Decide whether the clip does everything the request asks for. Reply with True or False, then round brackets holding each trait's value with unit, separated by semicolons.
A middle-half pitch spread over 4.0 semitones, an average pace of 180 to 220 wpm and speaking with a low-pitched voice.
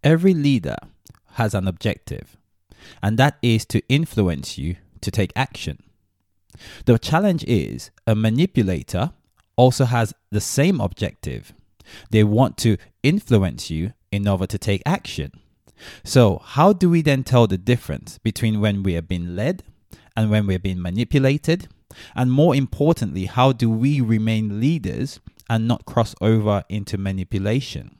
False (4.9 semitones; 145 wpm; 110 Hz)